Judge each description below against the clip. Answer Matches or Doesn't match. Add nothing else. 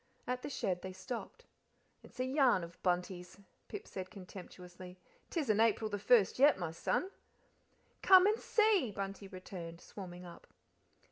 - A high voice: Matches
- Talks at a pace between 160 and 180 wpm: Doesn't match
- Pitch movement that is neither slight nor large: Doesn't match